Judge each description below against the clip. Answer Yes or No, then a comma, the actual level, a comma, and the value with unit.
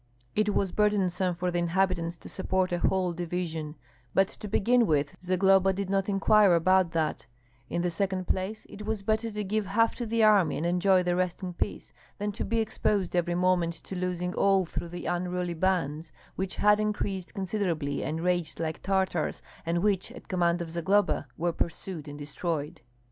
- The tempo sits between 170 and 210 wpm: Yes, average, 185 wpm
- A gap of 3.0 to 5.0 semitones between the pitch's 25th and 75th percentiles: No, narrow, 2.5 semitones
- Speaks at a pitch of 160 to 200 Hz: Yes, medium, 185 Hz